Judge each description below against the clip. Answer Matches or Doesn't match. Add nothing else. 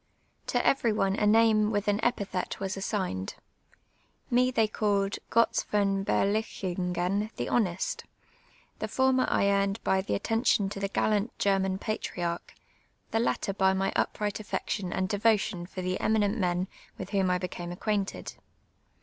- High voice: Matches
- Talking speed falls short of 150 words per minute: Doesn't match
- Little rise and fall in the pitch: Matches